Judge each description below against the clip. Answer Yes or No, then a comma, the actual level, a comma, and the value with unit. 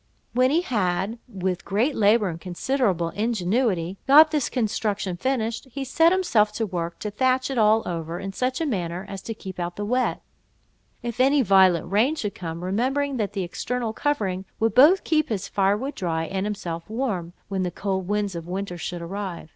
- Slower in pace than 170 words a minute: No, average, 185 wpm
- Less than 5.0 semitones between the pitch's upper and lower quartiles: No, wide, 5.5 semitones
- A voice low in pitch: No, high, 205 Hz